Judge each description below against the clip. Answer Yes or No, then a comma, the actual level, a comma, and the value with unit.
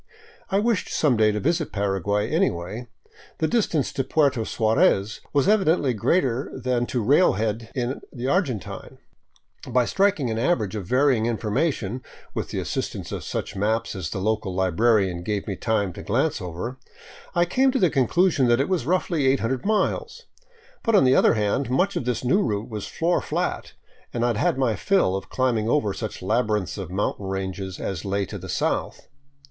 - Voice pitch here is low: Yes, low, 120 Hz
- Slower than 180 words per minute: No, average, 185 wpm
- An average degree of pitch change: No, wide, 6.4 semitones